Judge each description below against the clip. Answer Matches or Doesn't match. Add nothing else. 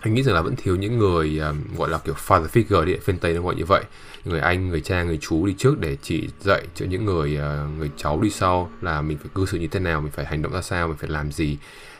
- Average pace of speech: Doesn't match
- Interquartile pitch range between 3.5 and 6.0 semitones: Matches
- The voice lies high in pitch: Doesn't match